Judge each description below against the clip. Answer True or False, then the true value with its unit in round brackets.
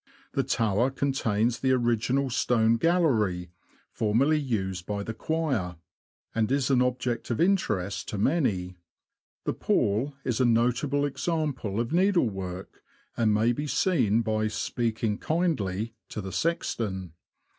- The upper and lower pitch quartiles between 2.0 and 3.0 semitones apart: False (4.9 semitones)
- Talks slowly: True (130 wpm)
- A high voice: False (115 Hz)